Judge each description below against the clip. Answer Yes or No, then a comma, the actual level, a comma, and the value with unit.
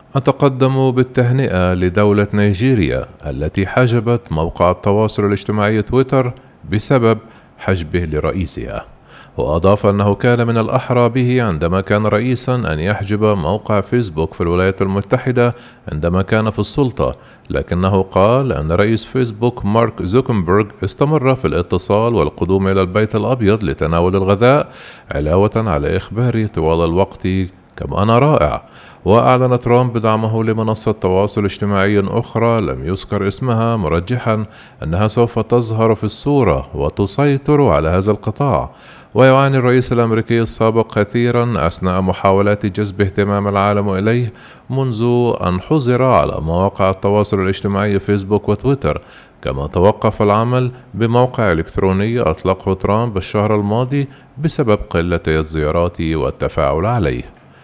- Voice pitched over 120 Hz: No, low, 105 Hz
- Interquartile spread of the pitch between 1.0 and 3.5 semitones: No, average, 4.1 semitones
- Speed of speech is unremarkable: Yes, average, 115 wpm